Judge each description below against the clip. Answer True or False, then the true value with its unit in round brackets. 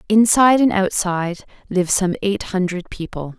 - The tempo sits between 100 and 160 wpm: True (140 wpm)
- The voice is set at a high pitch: True (195 Hz)